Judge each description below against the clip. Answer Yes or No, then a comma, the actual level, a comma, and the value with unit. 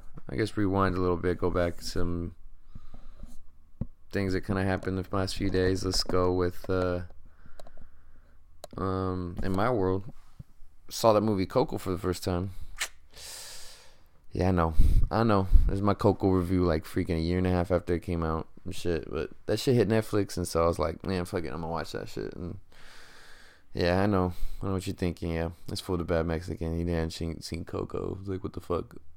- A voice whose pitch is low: Yes, very low, 90 Hz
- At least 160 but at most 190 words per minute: No, fast, 205 wpm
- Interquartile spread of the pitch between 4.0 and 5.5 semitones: No, narrow, 2.6 semitones